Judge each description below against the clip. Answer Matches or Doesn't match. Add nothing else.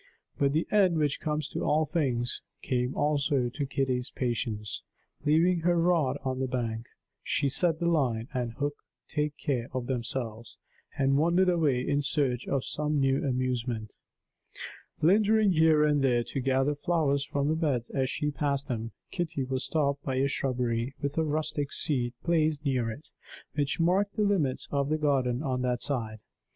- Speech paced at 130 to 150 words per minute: Doesn't match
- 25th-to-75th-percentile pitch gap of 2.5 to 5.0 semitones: Matches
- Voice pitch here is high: Doesn't match